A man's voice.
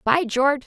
No: female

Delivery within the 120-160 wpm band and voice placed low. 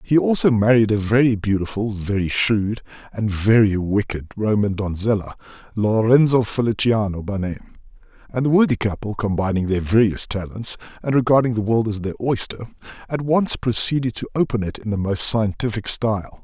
Yes: average, 155 wpm; low, 110 Hz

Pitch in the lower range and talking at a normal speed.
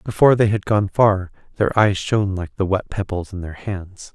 No: low, 100 Hz; fast, 215 wpm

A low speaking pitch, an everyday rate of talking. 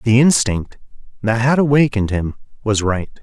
Yes: low, 115 Hz; average, 150 wpm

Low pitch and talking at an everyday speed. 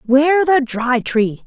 No: very high, 260 Hz; average, 165 wpm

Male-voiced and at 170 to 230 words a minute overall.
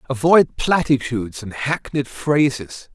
No: male; slow, 100 wpm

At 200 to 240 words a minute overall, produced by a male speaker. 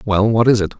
No: fast, 300 wpm; male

